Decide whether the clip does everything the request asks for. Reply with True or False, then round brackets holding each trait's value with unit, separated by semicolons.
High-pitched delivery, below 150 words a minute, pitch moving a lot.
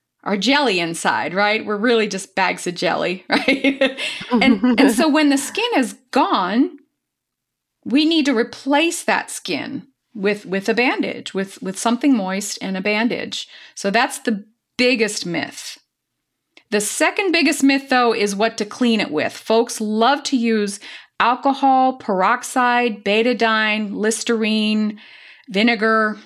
False (235 Hz; 140 wpm; 4.2 semitones)